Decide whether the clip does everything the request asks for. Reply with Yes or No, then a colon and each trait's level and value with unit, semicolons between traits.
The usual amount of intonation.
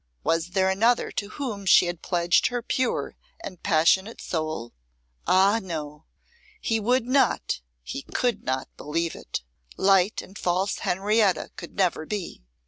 Yes: average, 4.2 semitones